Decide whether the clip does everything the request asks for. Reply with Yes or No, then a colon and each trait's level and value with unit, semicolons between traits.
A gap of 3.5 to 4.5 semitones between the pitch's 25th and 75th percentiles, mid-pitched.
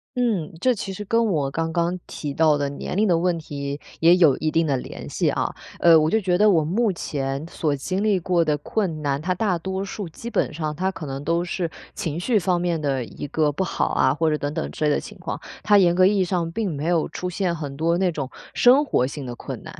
Yes: average, 4.0 semitones; medium, 170 Hz